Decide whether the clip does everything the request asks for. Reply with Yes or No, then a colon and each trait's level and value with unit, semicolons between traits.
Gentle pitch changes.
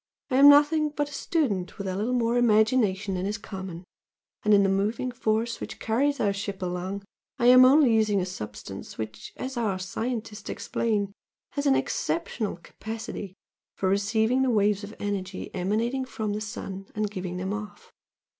No: average, 3.9 semitones